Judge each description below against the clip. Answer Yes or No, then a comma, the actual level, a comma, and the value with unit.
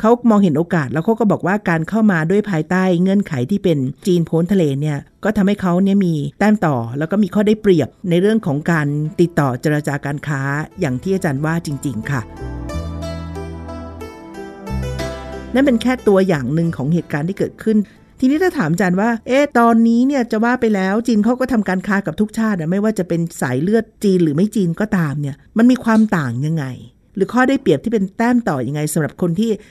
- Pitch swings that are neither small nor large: No, wide, 6.5 semitones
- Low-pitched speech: No, medium, 180 Hz